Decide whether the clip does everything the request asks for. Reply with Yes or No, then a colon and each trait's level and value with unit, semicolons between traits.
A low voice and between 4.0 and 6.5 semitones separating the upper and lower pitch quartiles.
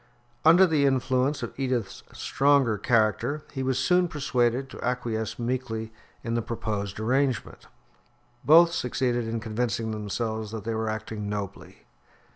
No: low, 120 Hz; average, 3.3 semitones